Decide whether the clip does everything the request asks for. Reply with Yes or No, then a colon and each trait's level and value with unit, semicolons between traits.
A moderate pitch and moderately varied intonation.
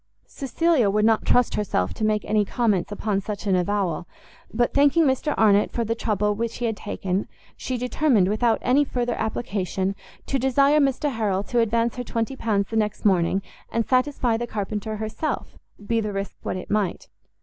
No: high, 220 Hz; average, 3.3 semitones